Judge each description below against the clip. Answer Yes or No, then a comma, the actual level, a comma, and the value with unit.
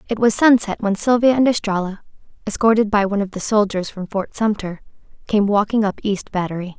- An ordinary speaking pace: Yes, average, 185 wpm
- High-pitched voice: Yes, high, 205 Hz